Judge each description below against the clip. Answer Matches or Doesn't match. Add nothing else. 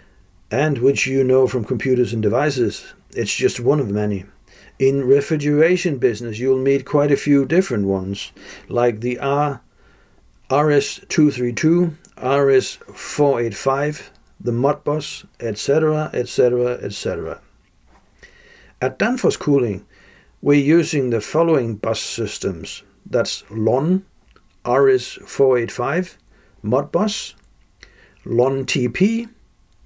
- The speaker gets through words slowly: Matches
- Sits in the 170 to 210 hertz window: Doesn't match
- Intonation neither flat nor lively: Matches